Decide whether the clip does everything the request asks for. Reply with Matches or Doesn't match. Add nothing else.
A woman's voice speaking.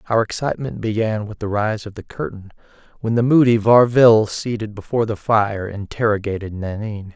Doesn't match